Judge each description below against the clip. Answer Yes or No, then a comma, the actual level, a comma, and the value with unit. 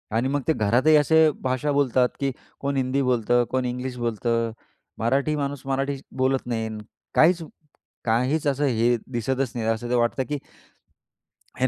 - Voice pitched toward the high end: No, low, 130 Hz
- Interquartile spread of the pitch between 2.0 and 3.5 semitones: Yes, average, 2.8 semitones